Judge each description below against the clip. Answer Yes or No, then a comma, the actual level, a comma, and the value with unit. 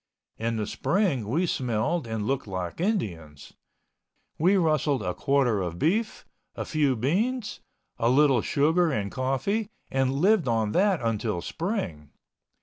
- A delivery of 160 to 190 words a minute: No, average, 140 wpm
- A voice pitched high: No, low, 135 Hz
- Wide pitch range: Yes, wide, 8.2 semitones